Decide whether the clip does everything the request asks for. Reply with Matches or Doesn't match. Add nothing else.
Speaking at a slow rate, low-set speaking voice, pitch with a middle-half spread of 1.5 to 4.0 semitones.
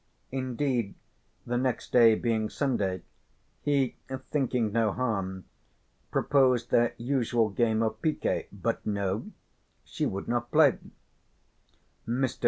Matches